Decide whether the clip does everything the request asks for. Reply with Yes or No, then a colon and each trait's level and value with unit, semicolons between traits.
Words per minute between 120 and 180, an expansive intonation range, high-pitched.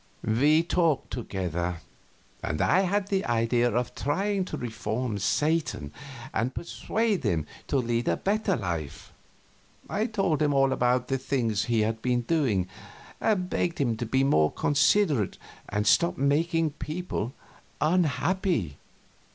No: slow, 135 wpm; wide, 7.2 semitones; low, 135 Hz